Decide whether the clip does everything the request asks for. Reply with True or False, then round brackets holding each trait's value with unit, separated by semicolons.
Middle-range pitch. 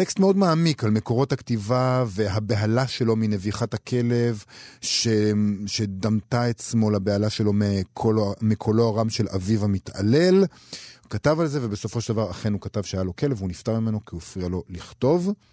False (110 Hz)